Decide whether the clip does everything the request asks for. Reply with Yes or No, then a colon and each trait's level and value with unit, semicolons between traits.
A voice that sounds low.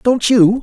No: high, 230 Hz